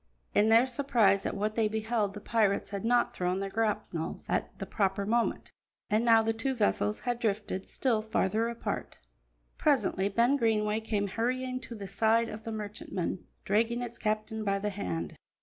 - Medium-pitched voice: No, high, 220 Hz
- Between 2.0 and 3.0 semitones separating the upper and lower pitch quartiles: Yes, narrow, 2.4 semitones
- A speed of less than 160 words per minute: No, average, 175 wpm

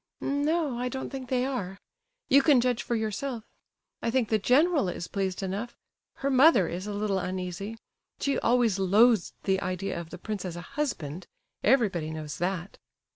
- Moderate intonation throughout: No, wide, 5.7 semitones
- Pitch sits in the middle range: No, high, 215 Hz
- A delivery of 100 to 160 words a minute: No, average, 180 wpm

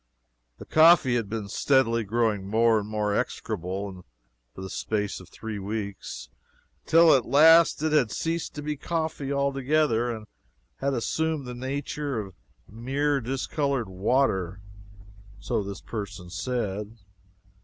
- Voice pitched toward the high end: No, low, 120 Hz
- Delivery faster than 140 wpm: No, slow, 135 wpm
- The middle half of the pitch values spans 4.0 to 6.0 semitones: Yes, wide, 5.4 semitones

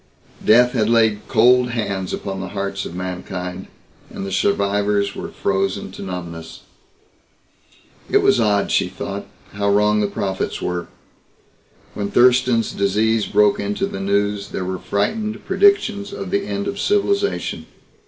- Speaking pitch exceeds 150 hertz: No, low, 100 Hz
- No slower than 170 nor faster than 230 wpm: No, average, 145 wpm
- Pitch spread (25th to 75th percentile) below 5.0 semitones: Yes, average, 2.8 semitones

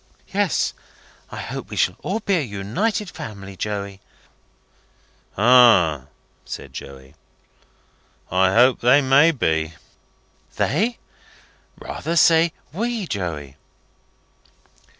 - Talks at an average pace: No, slow, 95 wpm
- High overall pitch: No, low, 115 Hz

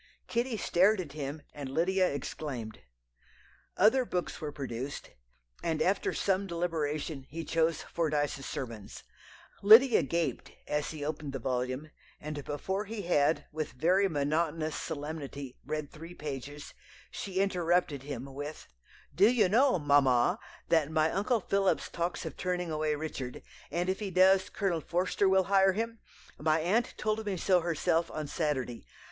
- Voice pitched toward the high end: No, medium, 160 Hz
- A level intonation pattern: No, average, 4.6 semitones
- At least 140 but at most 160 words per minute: Yes, average, 145 wpm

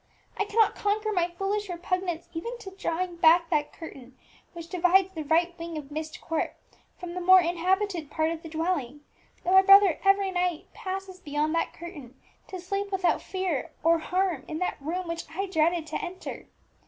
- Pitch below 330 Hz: No, very high, 350 Hz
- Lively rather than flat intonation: No, average, 2.9 semitones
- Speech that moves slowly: No, average, 180 wpm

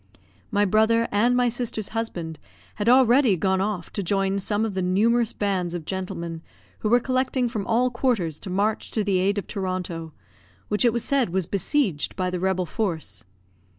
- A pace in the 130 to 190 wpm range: Yes, average, 185 wpm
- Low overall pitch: No, high, 205 Hz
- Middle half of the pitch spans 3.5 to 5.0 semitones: Yes, average, 4.1 semitones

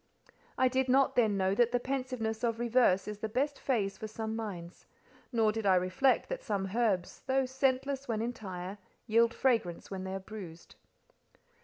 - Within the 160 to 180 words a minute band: Yes, average, 170 wpm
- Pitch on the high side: Yes, high, 225 Hz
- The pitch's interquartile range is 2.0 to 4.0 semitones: No, average, 4.5 semitones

